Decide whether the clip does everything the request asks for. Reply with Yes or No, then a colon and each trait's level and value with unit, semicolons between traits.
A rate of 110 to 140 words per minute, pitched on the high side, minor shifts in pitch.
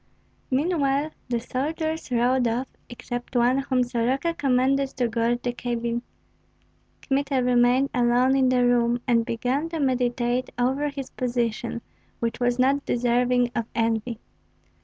Yes: slow, 135 wpm; very high, 250 Hz; narrow, 2.0 semitones